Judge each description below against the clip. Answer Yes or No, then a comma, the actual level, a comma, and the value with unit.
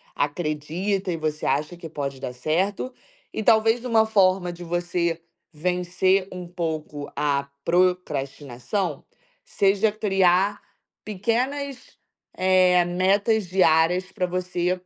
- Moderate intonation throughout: Yes, average, 3.5 semitones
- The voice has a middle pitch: Yes, medium, 180 Hz